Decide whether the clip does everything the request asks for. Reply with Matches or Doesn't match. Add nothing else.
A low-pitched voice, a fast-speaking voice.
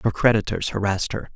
Doesn't match